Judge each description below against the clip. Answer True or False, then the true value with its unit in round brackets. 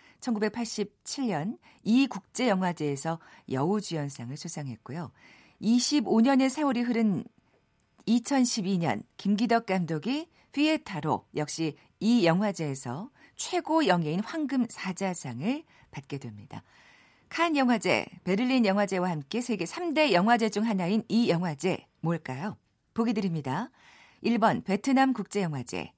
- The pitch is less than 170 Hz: False (205 Hz)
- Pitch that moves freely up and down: True (6.6 semitones)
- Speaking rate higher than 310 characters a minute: False (245 characters per minute)